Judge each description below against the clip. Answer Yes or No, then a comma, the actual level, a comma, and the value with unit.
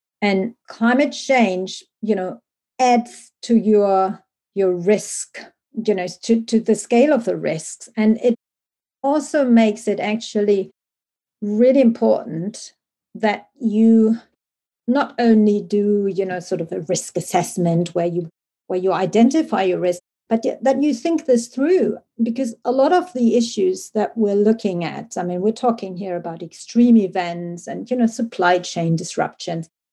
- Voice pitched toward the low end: No, high, 215 Hz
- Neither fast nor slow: Yes, average, 150 wpm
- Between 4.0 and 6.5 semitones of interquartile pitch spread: Yes, average, 4.3 semitones